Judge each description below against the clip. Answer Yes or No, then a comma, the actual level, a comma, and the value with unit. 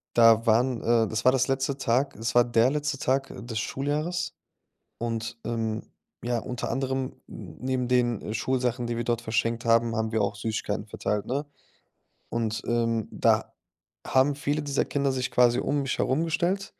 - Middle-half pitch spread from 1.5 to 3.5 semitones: Yes, average, 2.7 semitones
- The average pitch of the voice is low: Yes, low, 120 Hz